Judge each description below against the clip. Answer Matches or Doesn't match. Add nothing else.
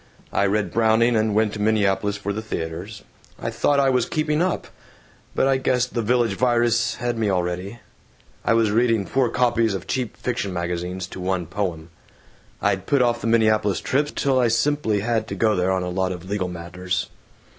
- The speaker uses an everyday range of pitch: Matches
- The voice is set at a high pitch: Doesn't match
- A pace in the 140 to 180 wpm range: Doesn't match